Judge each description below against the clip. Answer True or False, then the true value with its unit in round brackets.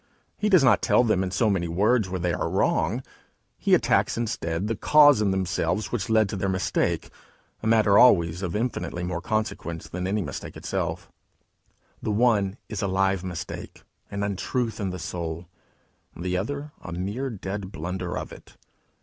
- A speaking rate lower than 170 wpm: False (175 wpm)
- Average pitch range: True (3.5 semitones)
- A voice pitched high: False (100 Hz)